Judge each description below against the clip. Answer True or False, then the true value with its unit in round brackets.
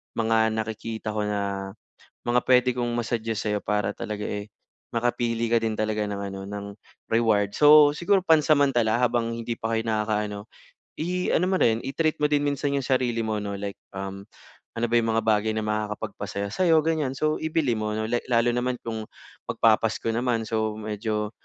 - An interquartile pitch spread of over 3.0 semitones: False (2.7 semitones)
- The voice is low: True (115 Hz)